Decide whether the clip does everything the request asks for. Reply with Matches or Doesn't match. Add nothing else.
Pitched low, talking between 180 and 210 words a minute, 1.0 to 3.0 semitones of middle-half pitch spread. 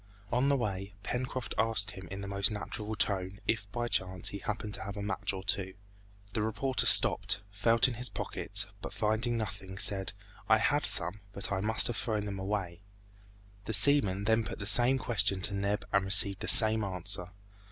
Matches